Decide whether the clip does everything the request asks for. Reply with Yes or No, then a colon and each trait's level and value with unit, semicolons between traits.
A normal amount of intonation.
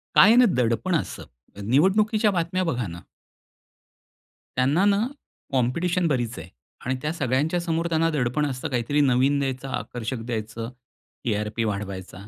No: wide, 6.4 semitones